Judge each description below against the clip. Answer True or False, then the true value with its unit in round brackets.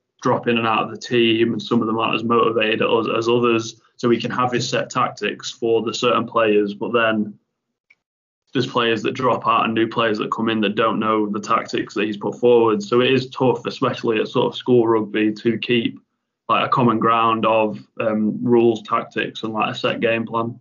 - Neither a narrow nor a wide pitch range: False (1.2 semitones)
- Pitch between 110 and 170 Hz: True (115 Hz)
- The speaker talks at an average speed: False (220 wpm)